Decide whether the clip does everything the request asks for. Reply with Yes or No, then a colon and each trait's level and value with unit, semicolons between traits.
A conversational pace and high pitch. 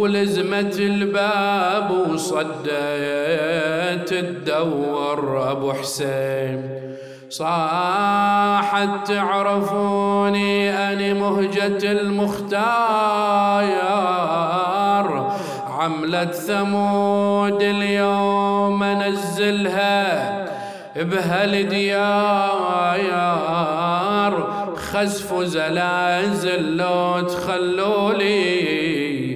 No: slow, 45 wpm; high, 200 Hz